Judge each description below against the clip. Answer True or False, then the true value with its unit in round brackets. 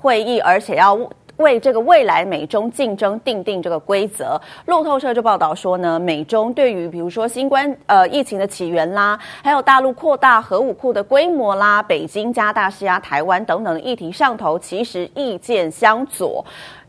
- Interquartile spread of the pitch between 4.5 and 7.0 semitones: True (5.4 semitones)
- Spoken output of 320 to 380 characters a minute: False (275 characters per minute)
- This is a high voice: True (220 Hz)